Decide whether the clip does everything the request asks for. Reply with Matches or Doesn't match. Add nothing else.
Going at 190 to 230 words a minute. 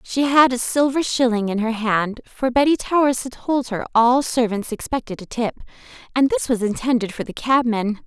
Matches